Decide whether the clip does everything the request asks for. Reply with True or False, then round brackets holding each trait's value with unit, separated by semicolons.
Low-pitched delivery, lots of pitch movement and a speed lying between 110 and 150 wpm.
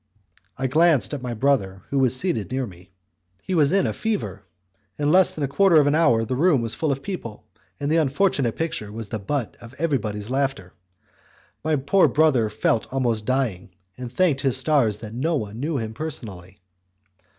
False (130 Hz; 5.7 semitones; 190 wpm)